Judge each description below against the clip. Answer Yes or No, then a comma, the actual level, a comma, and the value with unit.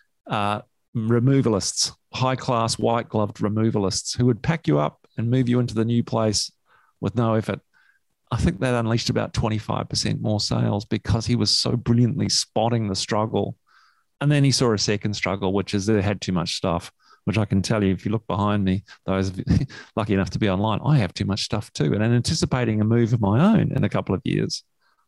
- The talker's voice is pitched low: Yes, low, 110 Hz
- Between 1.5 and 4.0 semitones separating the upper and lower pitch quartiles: Yes, average, 3.0 semitones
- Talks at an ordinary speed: No, fast, 210 wpm